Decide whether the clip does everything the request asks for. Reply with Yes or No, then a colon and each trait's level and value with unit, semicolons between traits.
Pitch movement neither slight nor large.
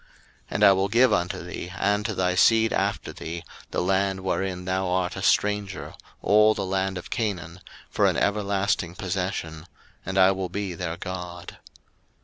No: narrow, 1.7 semitones